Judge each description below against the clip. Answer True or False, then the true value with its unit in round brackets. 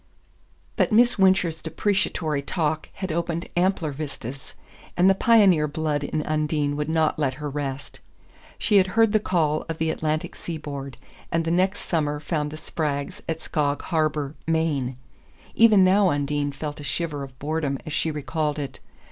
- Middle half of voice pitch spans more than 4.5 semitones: False (3.0 semitones)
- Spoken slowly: False (165 wpm)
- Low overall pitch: False (155 Hz)